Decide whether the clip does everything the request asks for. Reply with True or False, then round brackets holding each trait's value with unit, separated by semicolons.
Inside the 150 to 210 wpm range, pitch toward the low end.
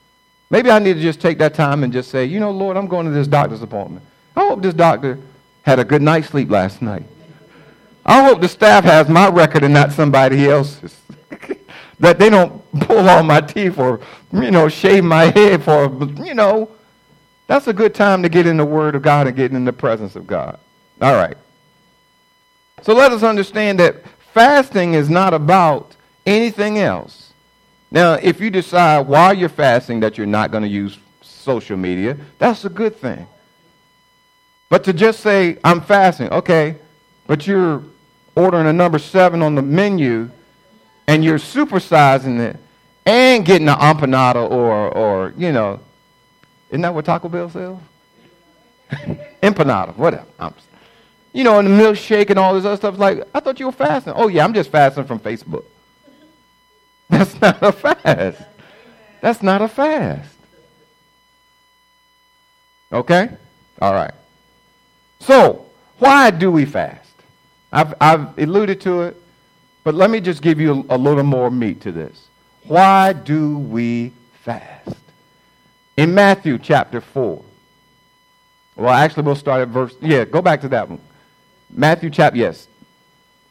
False (160 wpm; 165 Hz)